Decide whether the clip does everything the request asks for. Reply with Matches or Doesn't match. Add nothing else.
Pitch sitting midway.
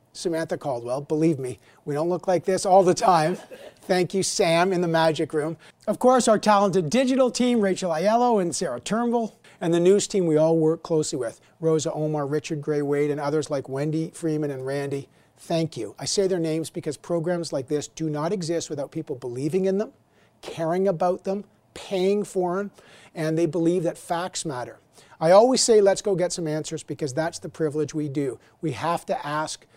Matches